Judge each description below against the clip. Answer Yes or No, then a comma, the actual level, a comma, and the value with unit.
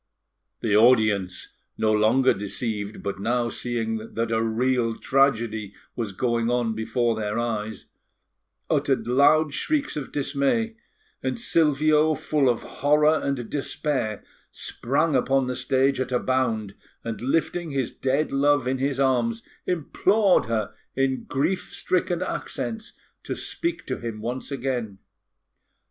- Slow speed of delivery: Yes, slow, 130 wpm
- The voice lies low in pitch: Yes, low, 130 Hz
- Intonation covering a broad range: No, average, 4.2 semitones